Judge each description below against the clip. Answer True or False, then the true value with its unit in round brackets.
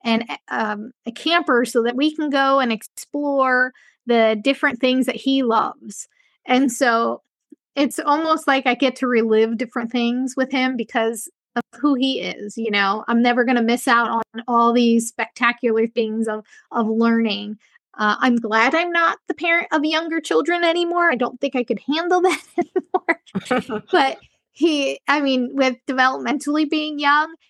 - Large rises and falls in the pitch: False (4.0 semitones)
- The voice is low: False (255 Hz)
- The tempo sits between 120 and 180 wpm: True (170 wpm)